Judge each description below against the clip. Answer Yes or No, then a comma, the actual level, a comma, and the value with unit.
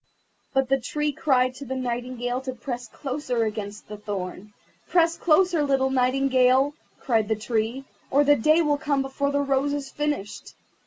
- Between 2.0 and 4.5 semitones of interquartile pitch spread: Yes, average, 3.0 semitones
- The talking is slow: No, average, 165 wpm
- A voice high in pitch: Yes, very high, 265 Hz